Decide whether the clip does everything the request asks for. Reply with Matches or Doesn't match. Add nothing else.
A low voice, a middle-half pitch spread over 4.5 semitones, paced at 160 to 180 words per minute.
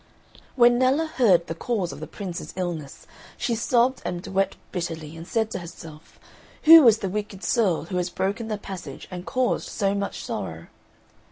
Doesn't match